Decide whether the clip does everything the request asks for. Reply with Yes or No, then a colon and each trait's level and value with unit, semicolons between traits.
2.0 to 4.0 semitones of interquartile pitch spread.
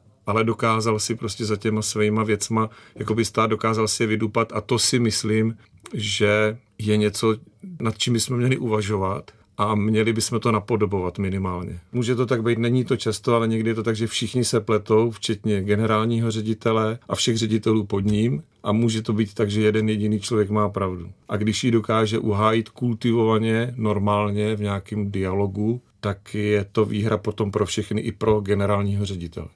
No: narrow, 1.5 semitones